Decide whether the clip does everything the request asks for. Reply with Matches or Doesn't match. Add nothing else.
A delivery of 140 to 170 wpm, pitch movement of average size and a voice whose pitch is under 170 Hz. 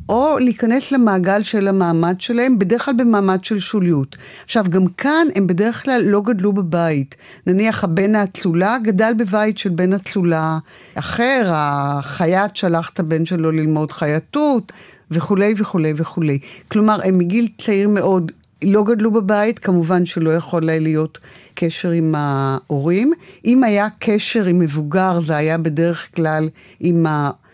Doesn't match